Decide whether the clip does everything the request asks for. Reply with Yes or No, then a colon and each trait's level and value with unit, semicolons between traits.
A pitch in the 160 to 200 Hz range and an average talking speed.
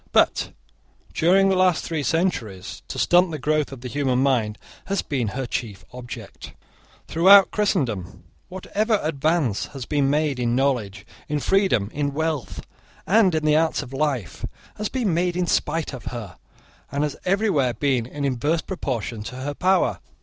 No: medium, 145 Hz; average, 165 wpm